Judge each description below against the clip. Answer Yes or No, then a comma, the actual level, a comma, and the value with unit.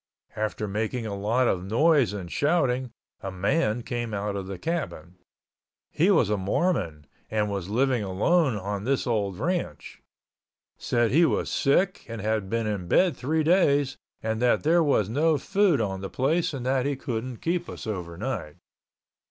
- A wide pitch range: Yes, wide, 6.4 semitones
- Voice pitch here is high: No, low, 120 Hz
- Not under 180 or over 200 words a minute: No, average, 170 wpm